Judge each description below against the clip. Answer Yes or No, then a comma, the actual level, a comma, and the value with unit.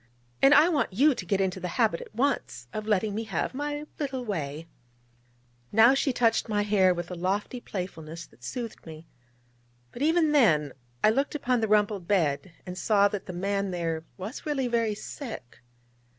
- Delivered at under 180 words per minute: No, average, 185 wpm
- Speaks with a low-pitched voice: No, high, 205 Hz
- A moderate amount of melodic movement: No, wide, 6.0 semitones